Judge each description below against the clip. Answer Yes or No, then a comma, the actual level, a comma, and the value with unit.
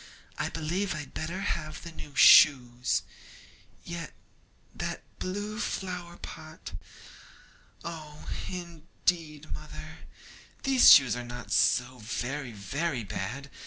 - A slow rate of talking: Yes, slow, 105 wpm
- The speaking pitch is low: No, medium, 155 Hz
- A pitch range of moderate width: Yes, average, 4.7 semitones